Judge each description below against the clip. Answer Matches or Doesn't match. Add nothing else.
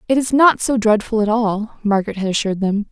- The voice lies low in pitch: Doesn't match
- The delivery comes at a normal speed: Doesn't match